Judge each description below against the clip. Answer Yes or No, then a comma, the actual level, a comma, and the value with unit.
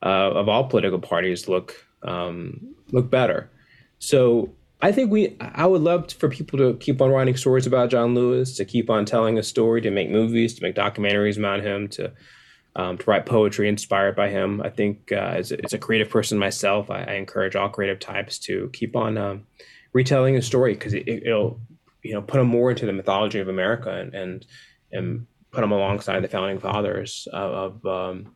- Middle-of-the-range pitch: No, low, 110 Hz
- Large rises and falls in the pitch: No, average, 4.1 semitones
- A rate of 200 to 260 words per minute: Yes, fast, 205 wpm